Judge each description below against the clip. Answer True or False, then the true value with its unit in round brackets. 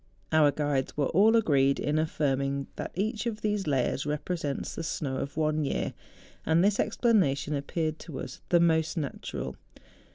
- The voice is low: False (155 Hz)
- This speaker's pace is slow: False (160 wpm)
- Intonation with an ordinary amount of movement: True (4.2 semitones)